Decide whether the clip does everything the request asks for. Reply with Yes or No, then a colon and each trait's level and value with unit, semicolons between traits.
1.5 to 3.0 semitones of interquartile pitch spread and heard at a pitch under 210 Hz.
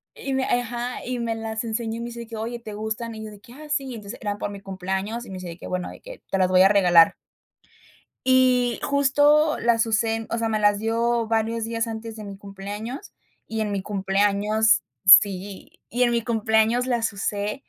No: narrow, 2.6 semitones; high, 225 Hz